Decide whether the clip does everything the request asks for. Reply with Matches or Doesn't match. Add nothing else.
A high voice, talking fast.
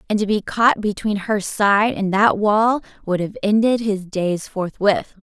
Doesn't match